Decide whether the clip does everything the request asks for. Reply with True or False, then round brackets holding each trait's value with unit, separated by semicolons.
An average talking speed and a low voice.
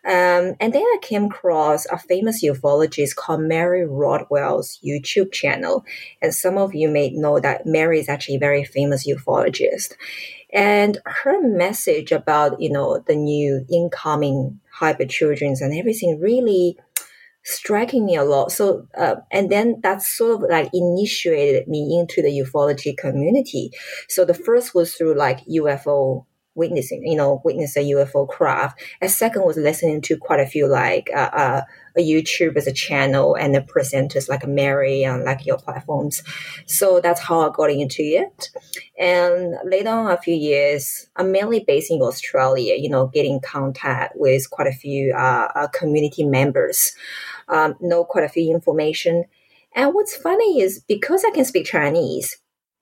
False (165 wpm; 165 Hz)